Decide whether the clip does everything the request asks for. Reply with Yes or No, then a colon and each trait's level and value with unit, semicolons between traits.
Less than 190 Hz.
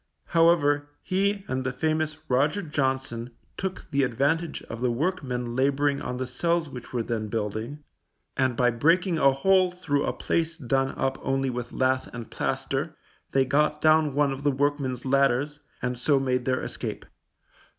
Yes: low, 135 Hz